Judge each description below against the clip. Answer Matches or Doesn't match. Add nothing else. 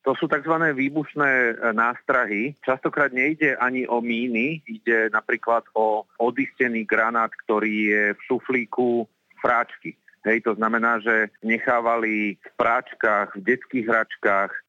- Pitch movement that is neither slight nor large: Matches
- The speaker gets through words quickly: Doesn't match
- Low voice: Matches